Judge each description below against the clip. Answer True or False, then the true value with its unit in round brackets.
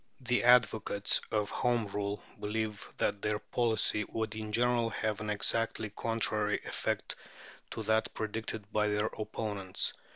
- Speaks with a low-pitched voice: True (110 Hz)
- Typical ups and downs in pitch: False (1.4 semitones)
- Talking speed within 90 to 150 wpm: True (135 wpm)